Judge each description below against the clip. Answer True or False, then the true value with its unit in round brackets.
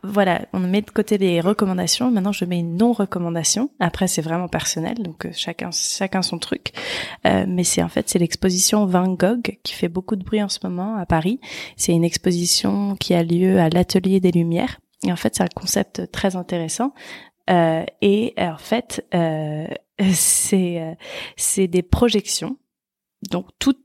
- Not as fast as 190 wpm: True (175 wpm)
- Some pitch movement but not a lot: True (3.1 semitones)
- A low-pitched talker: False (185 Hz)